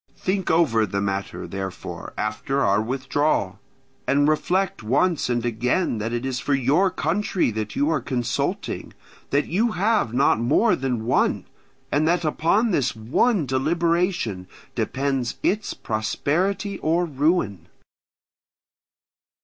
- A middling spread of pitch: No, wide, 7.0 semitones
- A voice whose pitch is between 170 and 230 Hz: No, medium, 140 Hz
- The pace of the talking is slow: Yes, slow, 125 wpm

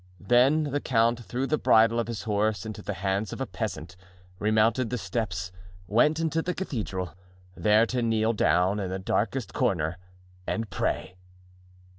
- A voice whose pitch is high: No, low, 110 Hz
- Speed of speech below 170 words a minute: Yes, average, 160 wpm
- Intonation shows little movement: No, average, 3.8 semitones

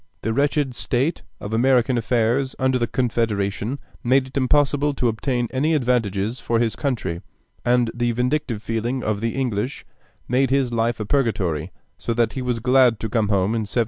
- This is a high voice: No, low, 120 Hz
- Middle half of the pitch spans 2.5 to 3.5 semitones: Yes, average, 2.8 semitones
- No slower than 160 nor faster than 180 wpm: Yes, average, 175 wpm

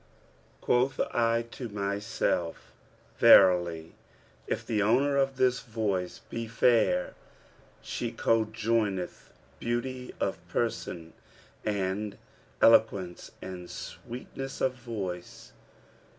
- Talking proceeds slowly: Yes, slow, 90 wpm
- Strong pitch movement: No, average, 4.3 semitones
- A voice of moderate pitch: No, low, 110 Hz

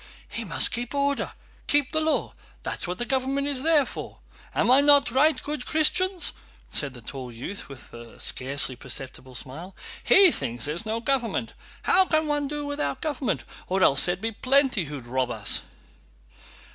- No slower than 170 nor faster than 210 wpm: Yes, average, 175 wpm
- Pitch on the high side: Yes, high, 235 Hz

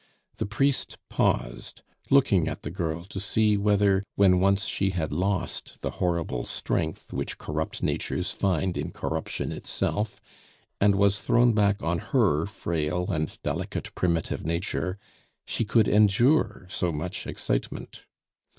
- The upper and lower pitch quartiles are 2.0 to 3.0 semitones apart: No, average, 3.5 semitones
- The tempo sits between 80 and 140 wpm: Yes, slow, 135 wpm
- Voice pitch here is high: No, very low, 95 Hz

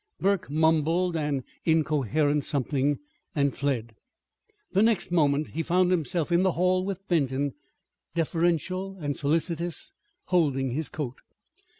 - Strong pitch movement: No, average, 3.8 semitones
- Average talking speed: No, slow, 120 wpm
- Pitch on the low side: No, medium, 160 Hz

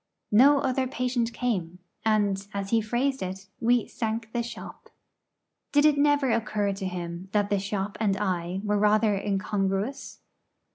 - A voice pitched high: Yes, high, 210 Hz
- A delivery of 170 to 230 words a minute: No, average, 150 wpm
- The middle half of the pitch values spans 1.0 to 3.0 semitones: No, average, 3.6 semitones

